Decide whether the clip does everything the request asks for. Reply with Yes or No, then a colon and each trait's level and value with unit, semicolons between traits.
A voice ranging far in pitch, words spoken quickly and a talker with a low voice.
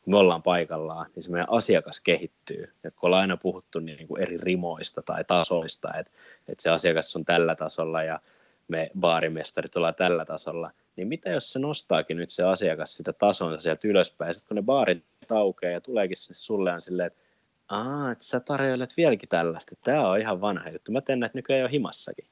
Yes: wide, 6.8 semitones; fast, 195 wpm; very low, 90 Hz